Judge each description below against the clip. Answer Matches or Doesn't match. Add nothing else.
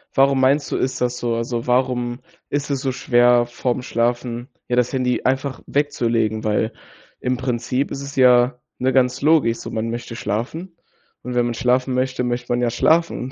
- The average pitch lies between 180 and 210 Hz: Doesn't match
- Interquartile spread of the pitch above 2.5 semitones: Doesn't match